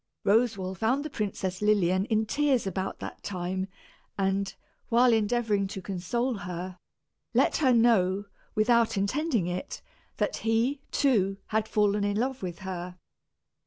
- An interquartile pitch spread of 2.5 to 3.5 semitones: No, average, 3.9 semitones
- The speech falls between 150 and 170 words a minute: No, slow, 135 wpm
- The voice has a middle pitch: No, high, 205 Hz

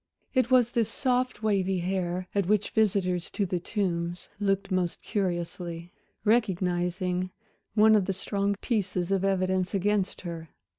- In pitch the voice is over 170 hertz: Yes, high, 190 Hz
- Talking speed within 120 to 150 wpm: Yes, average, 140 wpm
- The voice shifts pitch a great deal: No, narrow, 2.6 semitones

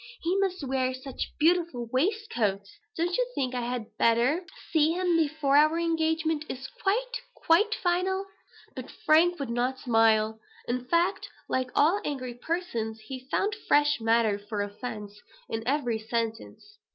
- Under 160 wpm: Yes, average, 145 wpm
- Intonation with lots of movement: Yes, wide, 6.5 semitones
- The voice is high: Yes, very high, 280 Hz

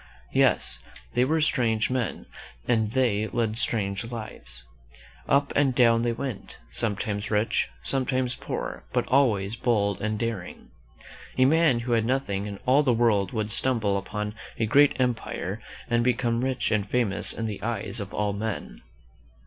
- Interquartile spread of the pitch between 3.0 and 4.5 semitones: Yes, average, 3.3 semitones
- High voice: No, low, 115 Hz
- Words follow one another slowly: No, average, 155 wpm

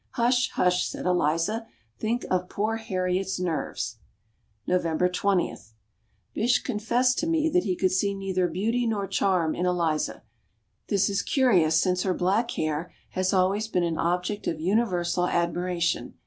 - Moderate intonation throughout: Yes, average, 3.5 semitones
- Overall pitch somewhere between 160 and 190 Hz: Yes, medium, 185 Hz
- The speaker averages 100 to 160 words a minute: Yes, average, 150 wpm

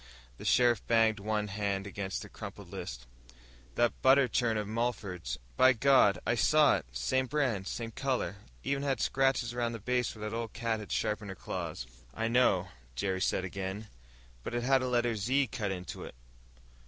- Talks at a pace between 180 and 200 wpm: Yes, average, 190 wpm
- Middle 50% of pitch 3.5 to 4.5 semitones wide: Yes, average, 3.9 semitones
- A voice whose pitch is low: Yes, low, 115 Hz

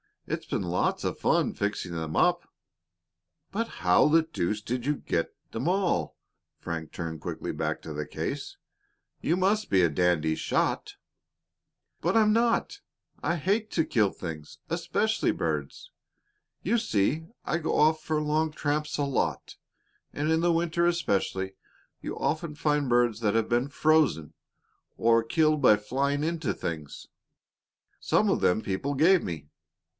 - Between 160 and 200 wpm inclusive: No, average, 150 wpm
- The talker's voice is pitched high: No, medium, 140 Hz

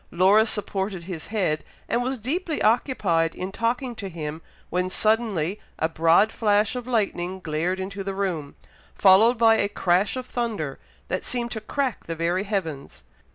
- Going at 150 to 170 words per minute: Yes, average, 160 wpm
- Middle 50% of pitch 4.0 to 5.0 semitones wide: Yes, average, 4.6 semitones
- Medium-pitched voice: No, high, 195 Hz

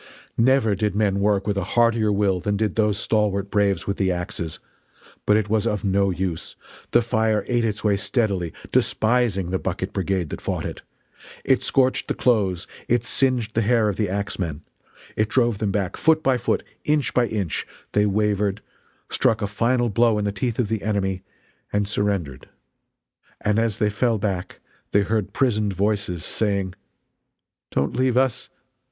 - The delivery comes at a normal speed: Yes, average, 170 wpm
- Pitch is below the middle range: Yes, low, 105 Hz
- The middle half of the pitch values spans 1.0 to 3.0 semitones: Yes, narrow, 2.6 semitones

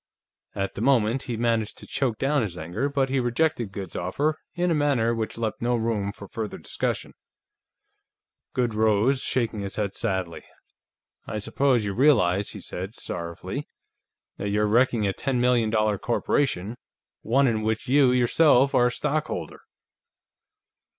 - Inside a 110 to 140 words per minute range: No, average, 155 wpm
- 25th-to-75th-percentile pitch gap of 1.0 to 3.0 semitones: No, average, 4.3 semitones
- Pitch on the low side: Yes, low, 115 Hz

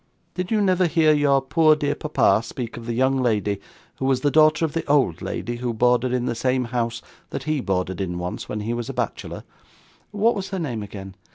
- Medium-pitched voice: No, low, 130 Hz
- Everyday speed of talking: No, fast, 220 wpm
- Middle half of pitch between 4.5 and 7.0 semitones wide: Yes, average, 5.1 semitones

